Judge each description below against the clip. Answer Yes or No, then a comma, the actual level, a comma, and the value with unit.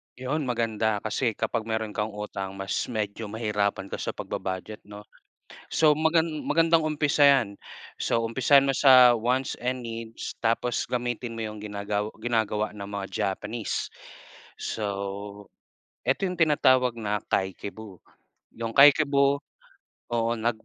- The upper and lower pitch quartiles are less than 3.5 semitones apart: No, average, 3.9 semitones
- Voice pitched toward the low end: Yes, low, 115 Hz